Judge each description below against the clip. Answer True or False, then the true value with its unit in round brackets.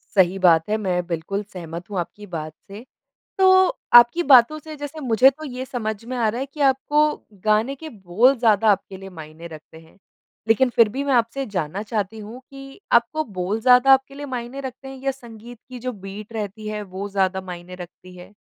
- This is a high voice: True (220 Hz)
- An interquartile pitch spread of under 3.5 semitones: False (5.6 semitones)